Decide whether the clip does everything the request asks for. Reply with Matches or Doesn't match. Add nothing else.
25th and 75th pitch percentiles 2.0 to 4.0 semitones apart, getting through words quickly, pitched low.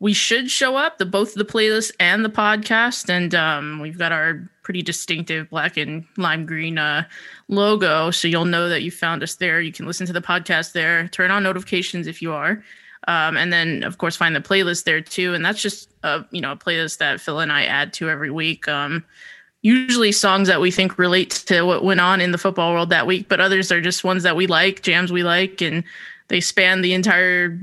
Doesn't match